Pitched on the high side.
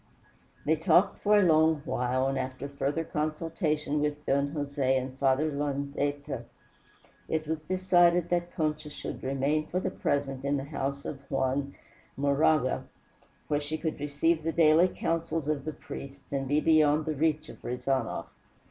No: medium, 150 Hz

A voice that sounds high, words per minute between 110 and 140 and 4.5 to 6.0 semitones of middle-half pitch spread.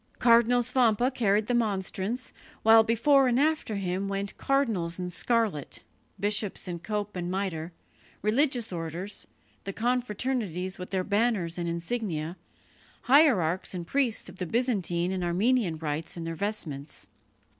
Yes: high, 200 Hz; slow, 135 wpm; average, 5.2 semitones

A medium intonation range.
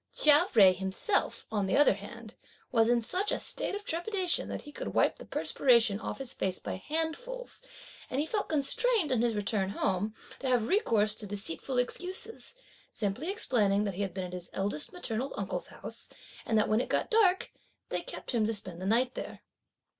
No: wide, 8.1 semitones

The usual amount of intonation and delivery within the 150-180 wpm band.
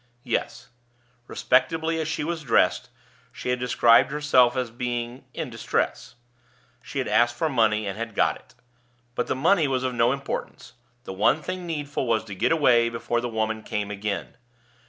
Yes: average, 4.2 semitones; average, 170 wpm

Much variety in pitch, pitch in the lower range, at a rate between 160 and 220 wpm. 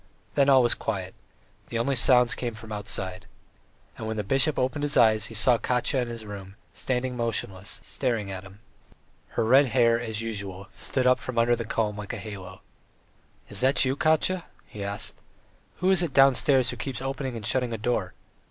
No: average, 3.7 semitones; low, 115 Hz; average, 190 wpm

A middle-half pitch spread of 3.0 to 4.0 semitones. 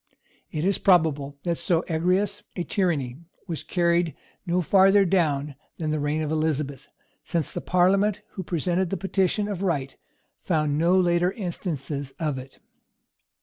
Yes: average, 3.6 semitones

